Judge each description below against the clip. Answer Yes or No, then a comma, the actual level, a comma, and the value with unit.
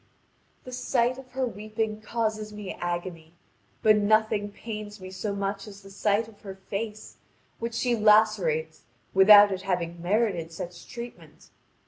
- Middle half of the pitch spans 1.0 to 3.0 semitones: Yes, narrow, 2.5 semitones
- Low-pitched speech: No, high, 210 Hz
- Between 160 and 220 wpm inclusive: No, average, 145 wpm